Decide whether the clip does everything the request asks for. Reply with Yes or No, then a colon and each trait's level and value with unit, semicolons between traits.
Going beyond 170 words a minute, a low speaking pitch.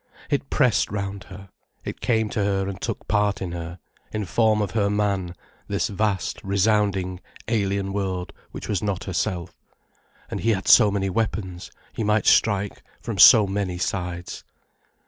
No: average, 160 wpm; low, 100 Hz